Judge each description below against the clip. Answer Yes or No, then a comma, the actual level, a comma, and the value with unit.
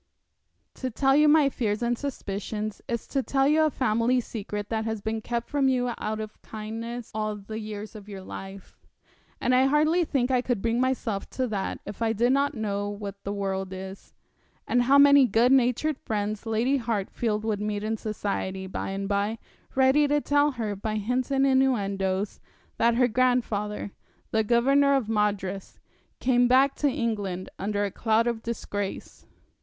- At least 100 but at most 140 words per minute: No, average, 175 wpm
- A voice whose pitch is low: No, high, 225 Hz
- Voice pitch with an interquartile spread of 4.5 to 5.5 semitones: No, average, 3.9 semitones